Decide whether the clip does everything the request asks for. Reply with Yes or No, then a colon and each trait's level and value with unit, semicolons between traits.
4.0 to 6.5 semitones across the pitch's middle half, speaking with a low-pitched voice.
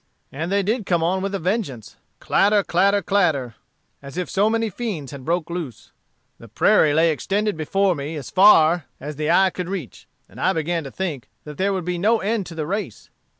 No: average, 4.6 semitones; medium, 175 Hz